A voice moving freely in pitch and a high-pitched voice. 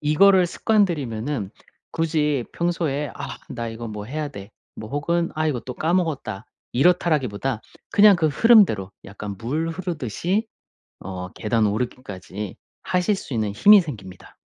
No: wide, 7.7 semitones; medium, 145 Hz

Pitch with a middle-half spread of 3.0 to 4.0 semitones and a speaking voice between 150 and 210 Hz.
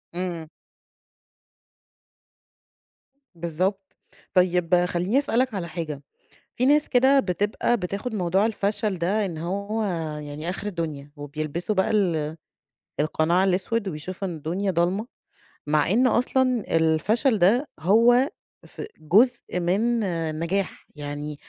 No: average, 4.8 semitones; medium, 185 Hz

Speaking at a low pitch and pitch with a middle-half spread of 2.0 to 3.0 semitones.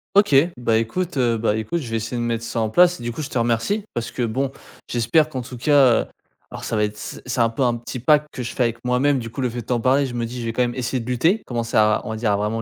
Yes: low, 120 Hz; narrow, 2.5 semitones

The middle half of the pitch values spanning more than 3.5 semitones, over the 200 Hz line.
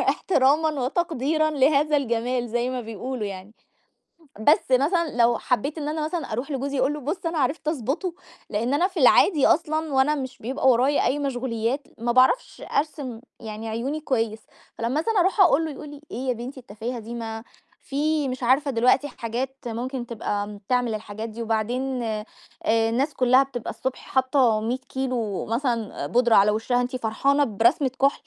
Yes: average, 3.9 semitones; very high, 255 Hz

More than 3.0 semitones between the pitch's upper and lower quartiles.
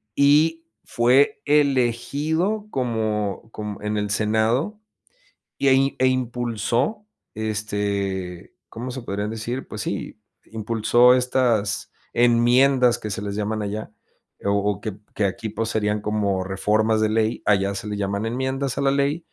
Yes: average, 3.8 semitones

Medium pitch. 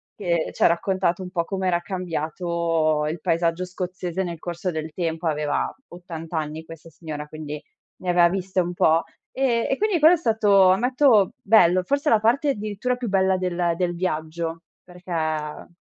Yes: medium, 175 Hz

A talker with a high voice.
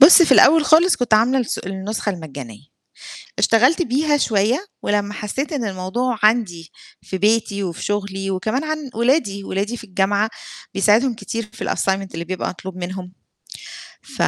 Yes: high, 210 Hz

